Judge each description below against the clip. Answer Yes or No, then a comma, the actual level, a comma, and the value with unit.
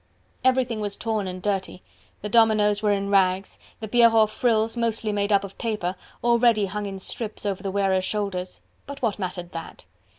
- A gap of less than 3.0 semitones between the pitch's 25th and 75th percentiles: Yes, narrow, 2.5 semitones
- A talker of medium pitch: No, high, 210 Hz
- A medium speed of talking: Yes, average, 175 wpm